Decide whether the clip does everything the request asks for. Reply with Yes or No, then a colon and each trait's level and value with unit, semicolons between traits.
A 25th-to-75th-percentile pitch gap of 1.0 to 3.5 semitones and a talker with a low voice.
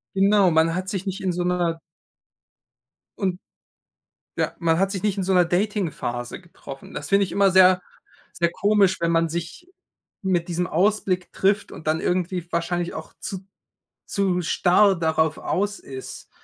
No: narrow, 2.4 semitones; medium, 180 Hz